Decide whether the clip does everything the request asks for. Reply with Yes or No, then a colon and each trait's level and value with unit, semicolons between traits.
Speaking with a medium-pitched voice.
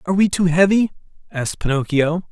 Yes: medium, 170 Hz